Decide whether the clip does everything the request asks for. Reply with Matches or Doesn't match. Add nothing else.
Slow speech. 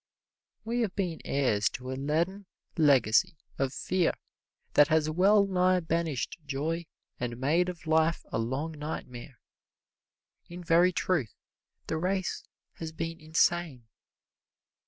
Matches